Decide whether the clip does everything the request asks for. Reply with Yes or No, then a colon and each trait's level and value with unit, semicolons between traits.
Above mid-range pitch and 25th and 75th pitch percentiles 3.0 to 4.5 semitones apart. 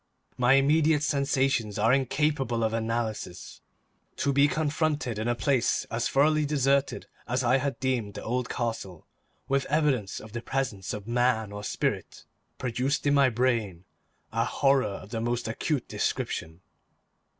No: low, 125 Hz; average, 3.8 semitones